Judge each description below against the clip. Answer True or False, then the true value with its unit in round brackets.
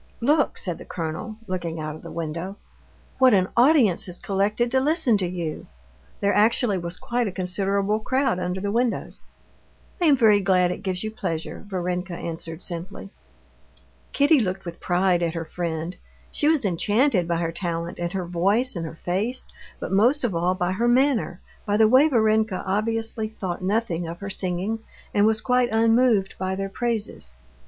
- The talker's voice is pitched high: True (195 Hz)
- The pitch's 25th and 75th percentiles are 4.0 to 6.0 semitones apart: True (4.3 semitones)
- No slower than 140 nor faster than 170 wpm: False (180 wpm)